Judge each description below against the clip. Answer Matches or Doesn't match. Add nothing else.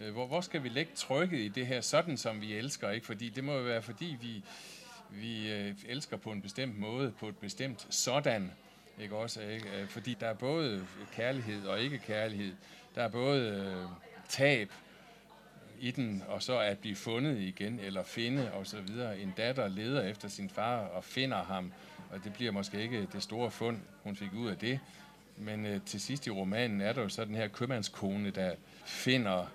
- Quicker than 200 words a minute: Doesn't match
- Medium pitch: Doesn't match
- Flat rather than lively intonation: Doesn't match